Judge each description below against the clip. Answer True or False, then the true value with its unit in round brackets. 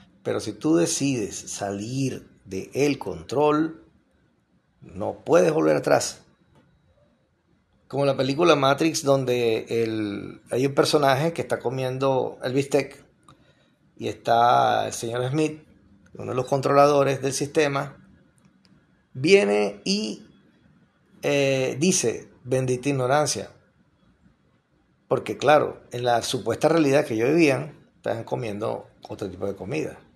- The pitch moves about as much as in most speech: True (3.8 semitones)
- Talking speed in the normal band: False (115 wpm)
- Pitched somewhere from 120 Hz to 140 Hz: True (135 Hz)